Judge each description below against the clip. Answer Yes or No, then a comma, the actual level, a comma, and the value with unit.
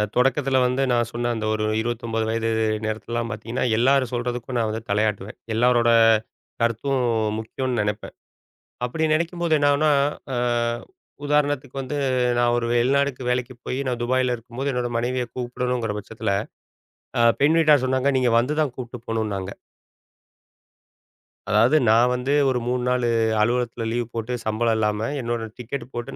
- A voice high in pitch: No, low, 120 Hz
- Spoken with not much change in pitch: Yes, narrow, 2.2 semitones